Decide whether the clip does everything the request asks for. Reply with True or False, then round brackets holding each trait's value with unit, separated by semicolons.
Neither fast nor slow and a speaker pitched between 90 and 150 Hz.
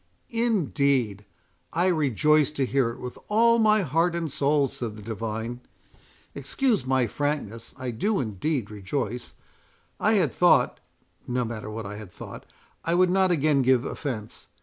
True (145 wpm; 135 Hz)